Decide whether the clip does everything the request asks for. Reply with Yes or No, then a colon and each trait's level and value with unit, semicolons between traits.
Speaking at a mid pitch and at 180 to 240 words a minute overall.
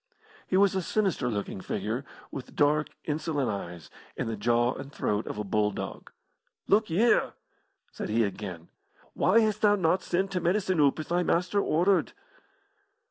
No: medium, 155 Hz; average, 160 wpm